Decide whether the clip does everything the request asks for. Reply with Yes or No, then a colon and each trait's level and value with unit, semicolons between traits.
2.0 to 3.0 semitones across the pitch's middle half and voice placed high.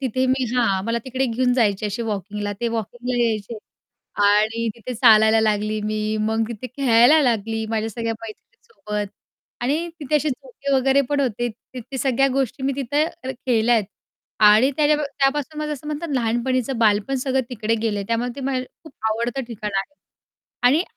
No: average, 3.7 semitones; high, 240 Hz